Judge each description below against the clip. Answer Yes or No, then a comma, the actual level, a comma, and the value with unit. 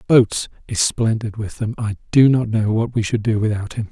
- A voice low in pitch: Yes, low, 110 Hz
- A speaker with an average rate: No, fast, 215 wpm